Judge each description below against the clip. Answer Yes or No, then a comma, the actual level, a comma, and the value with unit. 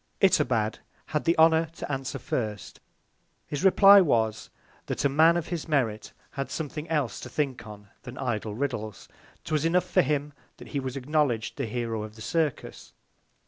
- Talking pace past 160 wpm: Yes, average, 170 wpm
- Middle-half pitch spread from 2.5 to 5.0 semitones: No, wide, 5.6 semitones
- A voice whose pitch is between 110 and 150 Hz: Yes, medium, 140 Hz